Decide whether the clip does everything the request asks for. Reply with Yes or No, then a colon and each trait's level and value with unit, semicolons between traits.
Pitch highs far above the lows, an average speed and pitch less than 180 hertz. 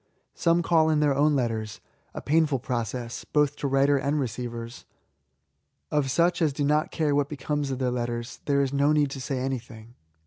No: average, 3.2 semitones; average, 195 wpm; medium, 140 Hz